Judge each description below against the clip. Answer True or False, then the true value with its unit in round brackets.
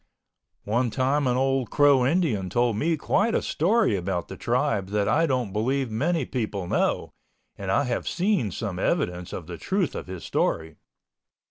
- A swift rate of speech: False (170 wpm)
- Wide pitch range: True (6.7 semitones)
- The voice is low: True (125 Hz)